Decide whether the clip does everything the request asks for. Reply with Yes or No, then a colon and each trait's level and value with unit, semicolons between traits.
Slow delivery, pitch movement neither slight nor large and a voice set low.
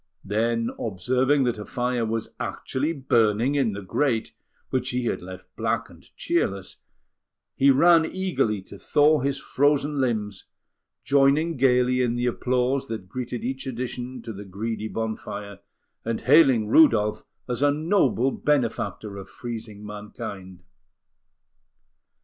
Yes: slow, 130 wpm; average, 4.1 semitones; low, 120 Hz